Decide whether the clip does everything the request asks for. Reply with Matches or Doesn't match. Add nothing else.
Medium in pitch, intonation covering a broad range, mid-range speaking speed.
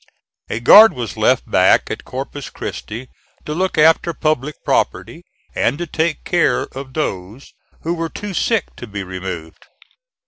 Matches